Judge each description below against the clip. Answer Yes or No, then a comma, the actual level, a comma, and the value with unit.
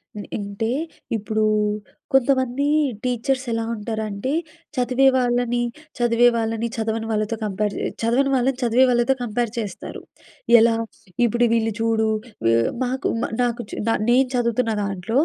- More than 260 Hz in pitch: No, high, 235 Hz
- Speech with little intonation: Yes, narrow, 2.0 semitones